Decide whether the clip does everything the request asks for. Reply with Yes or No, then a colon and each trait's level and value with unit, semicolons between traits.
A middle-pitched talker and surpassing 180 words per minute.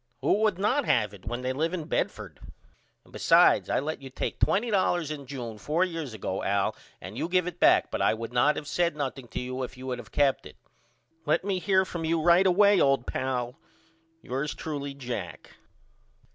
Yes: medium, 145 Hz; average, 200 wpm